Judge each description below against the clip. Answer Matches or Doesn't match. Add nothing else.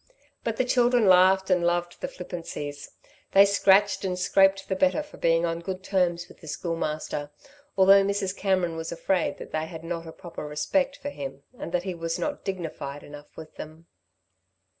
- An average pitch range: Matches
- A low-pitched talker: Doesn't match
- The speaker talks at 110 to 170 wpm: Doesn't match